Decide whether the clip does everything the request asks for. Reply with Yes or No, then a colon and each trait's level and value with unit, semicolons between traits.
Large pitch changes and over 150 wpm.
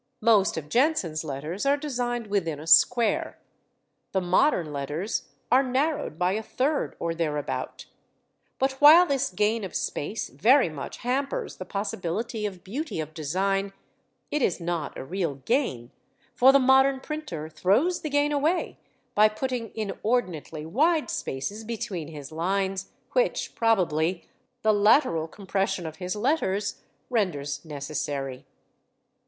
No: wide, 7.8 semitones; slow, 135 wpm